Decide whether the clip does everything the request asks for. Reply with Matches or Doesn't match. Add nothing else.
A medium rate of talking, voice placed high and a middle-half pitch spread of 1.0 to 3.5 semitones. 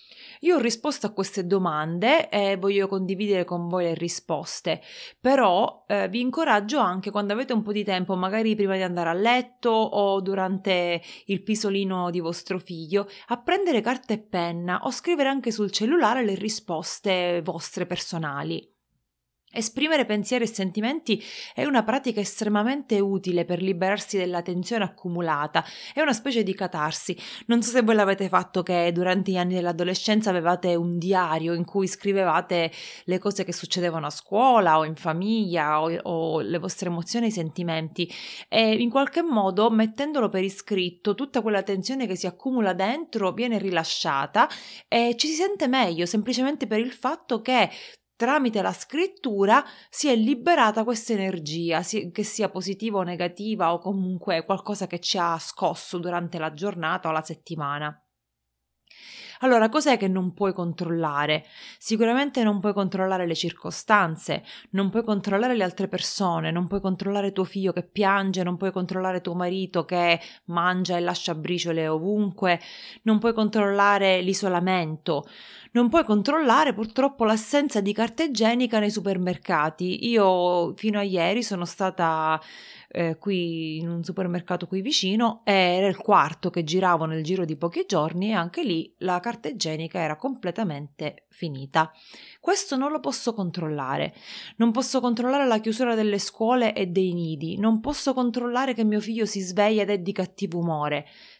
Doesn't match